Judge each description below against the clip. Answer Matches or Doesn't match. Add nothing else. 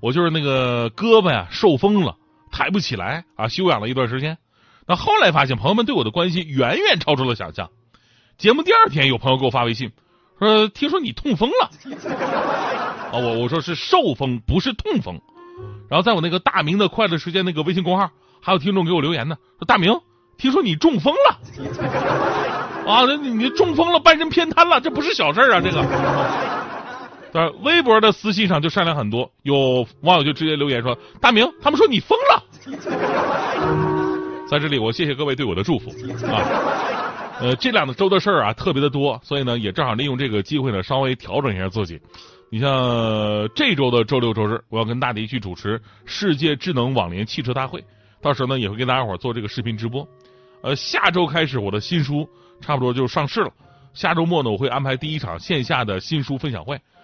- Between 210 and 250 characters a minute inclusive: Doesn't match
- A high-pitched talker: Doesn't match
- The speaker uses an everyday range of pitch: Doesn't match